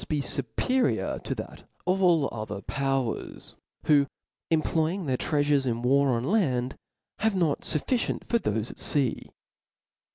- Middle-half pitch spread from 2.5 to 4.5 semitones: No, average, 5.1 semitones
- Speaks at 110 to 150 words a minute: No, average, 160 wpm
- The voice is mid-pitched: Yes, medium, 145 Hz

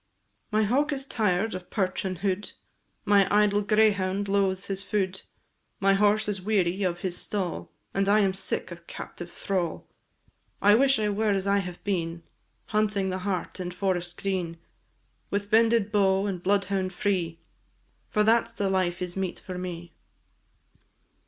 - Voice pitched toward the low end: No, high, 195 Hz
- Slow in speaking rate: No, average, 160 wpm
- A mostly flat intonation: Yes, narrow, 2.2 semitones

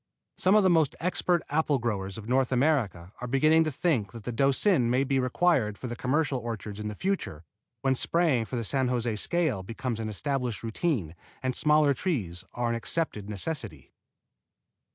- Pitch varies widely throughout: Yes, wide, 5.8 semitones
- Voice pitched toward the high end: No, low, 125 Hz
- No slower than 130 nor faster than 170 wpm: No, average, 180 wpm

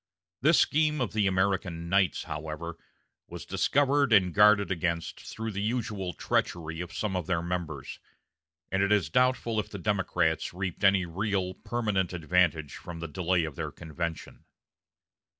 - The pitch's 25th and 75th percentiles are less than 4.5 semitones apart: Yes, average, 3.9 semitones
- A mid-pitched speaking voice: No, very low, 95 Hz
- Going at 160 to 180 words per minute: No, average, 150 wpm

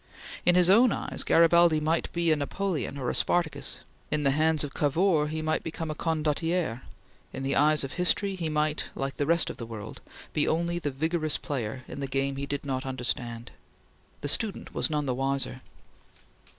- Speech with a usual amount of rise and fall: Yes, average, 3.5 semitones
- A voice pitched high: No, medium, 150 Hz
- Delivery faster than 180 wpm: Yes, average, 190 wpm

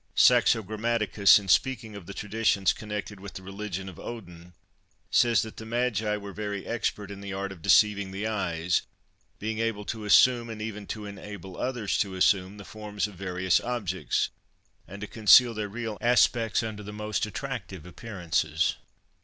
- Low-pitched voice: Yes, low, 105 Hz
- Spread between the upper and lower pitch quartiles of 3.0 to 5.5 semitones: No, narrow, 2.5 semitones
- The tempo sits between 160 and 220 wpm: Yes, average, 170 wpm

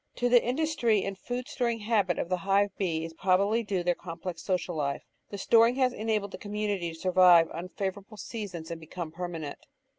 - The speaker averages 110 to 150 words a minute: No, average, 190 wpm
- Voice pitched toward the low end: No, high, 195 Hz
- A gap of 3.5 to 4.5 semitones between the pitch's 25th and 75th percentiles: Yes, average, 4.0 semitones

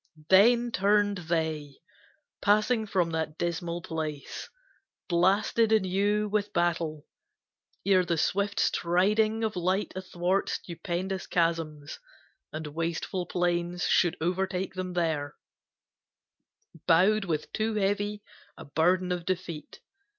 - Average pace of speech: No, slow, 105 wpm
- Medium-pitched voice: Yes, medium, 180 Hz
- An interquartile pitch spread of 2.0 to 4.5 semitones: Yes, average, 3.3 semitones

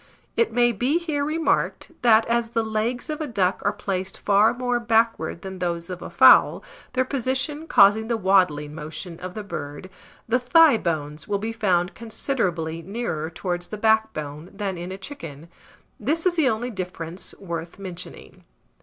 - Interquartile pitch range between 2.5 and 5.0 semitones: No, wide, 5.4 semitones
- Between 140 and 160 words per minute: No, average, 170 wpm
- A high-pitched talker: Yes, high, 205 Hz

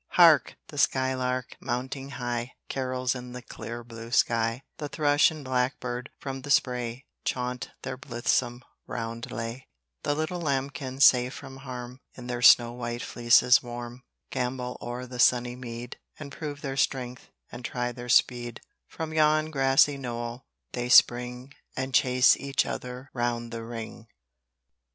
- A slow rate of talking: No, average, 145 wpm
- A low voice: Yes, low, 125 Hz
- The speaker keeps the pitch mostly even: Yes, narrow, 1.7 semitones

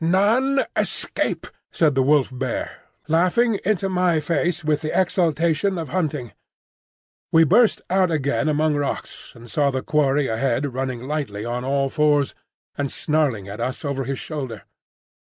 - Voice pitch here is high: No, medium, 150 Hz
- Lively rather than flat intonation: No, average, 4.2 semitones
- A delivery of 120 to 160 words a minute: Yes, average, 150 wpm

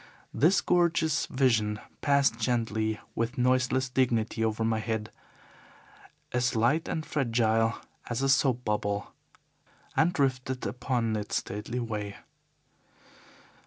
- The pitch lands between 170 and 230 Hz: No, low, 120 Hz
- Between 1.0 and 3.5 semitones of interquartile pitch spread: Yes, average, 3.2 semitones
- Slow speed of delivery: Yes, slow, 110 wpm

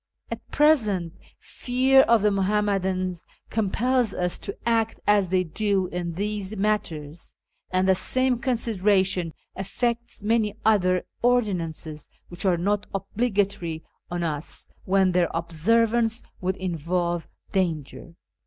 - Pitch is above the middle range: Yes, high, 195 Hz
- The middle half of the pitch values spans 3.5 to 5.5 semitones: Yes, average, 3.9 semitones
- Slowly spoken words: Yes, slow, 115 wpm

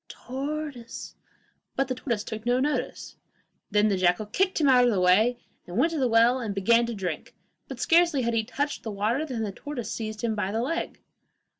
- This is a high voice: Yes, high, 235 Hz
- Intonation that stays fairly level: No, average, 4.2 semitones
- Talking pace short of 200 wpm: No, fast, 205 wpm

